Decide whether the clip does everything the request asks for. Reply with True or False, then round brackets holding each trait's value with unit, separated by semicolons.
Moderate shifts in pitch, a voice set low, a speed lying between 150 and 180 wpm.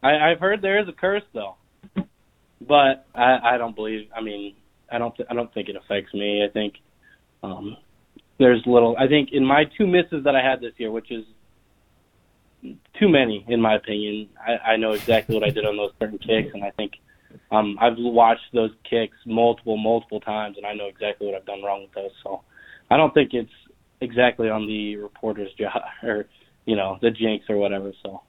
False (3.0 semitones; 110 Hz; 205 wpm)